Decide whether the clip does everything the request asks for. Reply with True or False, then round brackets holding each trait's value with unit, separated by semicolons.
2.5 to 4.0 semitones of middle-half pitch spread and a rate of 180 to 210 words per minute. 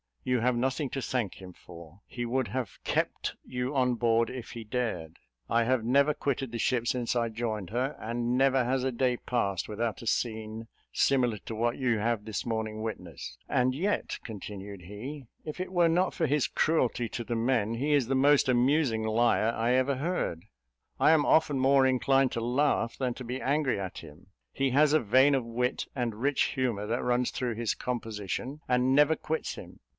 True (2.9 semitones; 195 wpm)